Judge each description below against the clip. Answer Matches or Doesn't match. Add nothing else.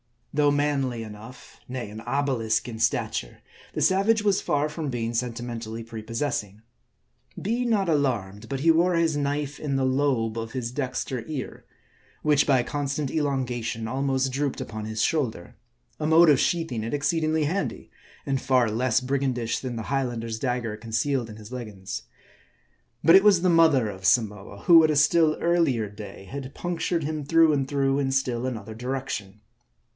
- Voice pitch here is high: Doesn't match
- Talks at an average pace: Matches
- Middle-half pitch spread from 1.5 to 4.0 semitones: Doesn't match